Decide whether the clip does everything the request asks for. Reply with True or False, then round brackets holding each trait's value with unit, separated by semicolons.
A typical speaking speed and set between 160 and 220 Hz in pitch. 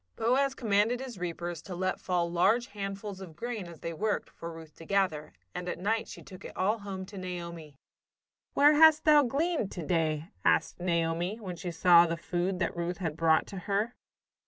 True (195 wpm; 185 Hz)